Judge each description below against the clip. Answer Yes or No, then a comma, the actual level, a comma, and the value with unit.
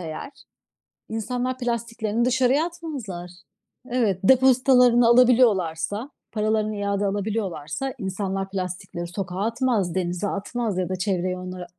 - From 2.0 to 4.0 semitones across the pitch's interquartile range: No, average, 4.8 semitones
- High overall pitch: Yes, high, 210 Hz